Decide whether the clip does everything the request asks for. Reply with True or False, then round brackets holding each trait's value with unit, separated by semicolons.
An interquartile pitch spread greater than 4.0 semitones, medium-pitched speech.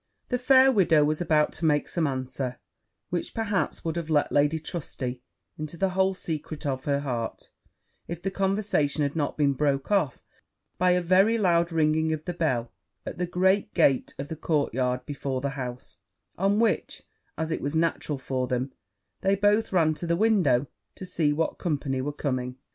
True (4.6 semitones; 155 Hz)